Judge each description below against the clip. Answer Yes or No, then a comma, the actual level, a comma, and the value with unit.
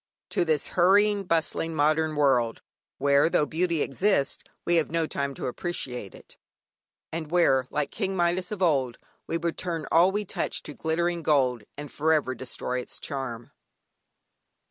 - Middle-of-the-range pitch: Yes, medium, 160 Hz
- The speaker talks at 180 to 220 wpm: No, average, 160 wpm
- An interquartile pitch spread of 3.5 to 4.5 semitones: Yes, average, 3.9 semitones